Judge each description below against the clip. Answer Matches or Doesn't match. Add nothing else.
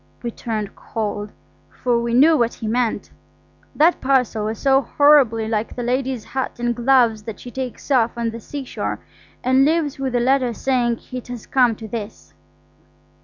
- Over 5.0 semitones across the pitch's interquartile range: Doesn't match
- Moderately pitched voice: Doesn't match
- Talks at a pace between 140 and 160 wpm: Doesn't match